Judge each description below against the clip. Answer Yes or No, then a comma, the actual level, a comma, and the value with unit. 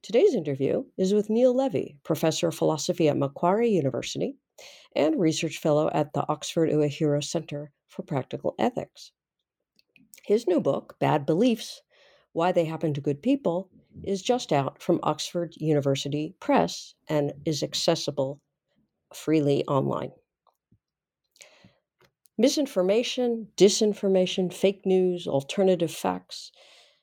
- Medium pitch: Yes, medium, 170 Hz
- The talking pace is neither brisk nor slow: No, slow, 115 wpm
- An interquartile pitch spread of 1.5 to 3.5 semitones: No, average, 5.3 semitones